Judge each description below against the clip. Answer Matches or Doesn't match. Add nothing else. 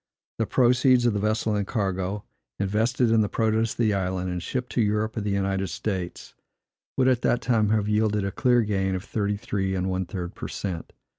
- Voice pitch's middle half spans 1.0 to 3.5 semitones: Matches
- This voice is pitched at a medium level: Doesn't match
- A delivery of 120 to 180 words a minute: Doesn't match